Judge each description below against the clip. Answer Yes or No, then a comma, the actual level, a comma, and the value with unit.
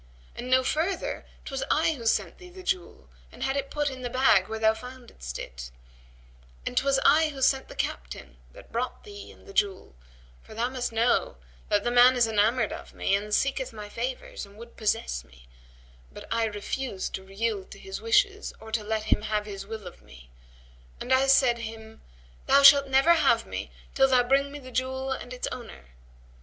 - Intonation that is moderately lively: Yes, average, 4.2 semitones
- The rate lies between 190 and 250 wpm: Yes, average, 200 wpm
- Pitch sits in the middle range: No, high, 240 Hz